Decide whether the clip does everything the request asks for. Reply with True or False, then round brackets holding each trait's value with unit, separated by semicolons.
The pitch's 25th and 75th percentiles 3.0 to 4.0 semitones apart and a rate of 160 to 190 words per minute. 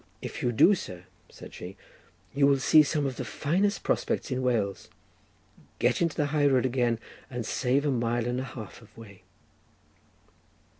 True (3.6 semitones; 170 wpm)